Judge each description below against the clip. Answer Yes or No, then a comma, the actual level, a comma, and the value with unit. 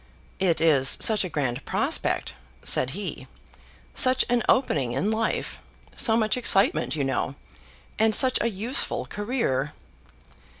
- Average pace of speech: No, slow, 130 wpm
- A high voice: Yes, high, 205 Hz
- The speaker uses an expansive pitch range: Yes, wide, 8.5 semitones